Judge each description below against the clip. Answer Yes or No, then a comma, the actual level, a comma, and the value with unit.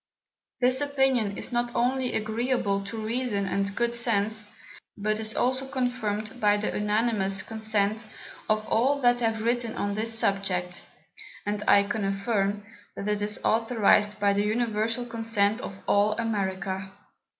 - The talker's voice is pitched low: No, high, 215 Hz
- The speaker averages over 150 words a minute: No, average, 145 wpm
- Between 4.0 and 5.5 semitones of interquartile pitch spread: No, average, 2.7 semitones